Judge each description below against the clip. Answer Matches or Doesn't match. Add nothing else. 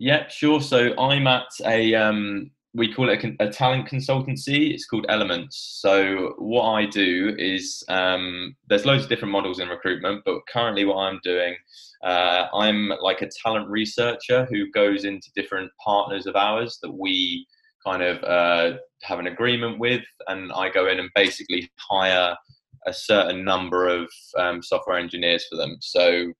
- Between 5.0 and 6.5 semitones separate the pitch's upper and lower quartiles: Matches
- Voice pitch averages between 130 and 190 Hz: Doesn't match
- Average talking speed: Matches